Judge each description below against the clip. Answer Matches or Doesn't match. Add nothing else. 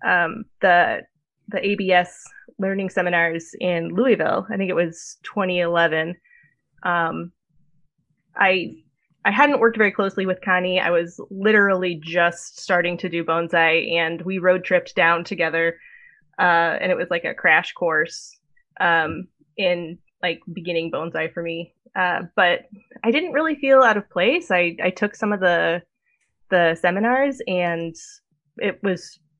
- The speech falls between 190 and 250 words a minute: Doesn't match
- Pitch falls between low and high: Matches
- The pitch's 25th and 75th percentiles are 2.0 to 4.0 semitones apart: Matches